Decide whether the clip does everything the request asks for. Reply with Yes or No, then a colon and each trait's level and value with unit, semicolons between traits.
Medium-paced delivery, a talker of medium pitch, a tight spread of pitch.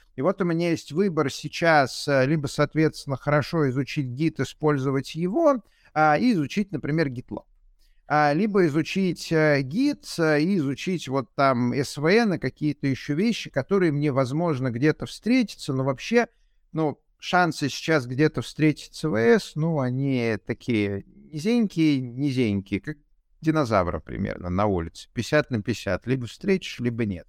No: average, 140 wpm; medium, 150 Hz; average, 4.2 semitones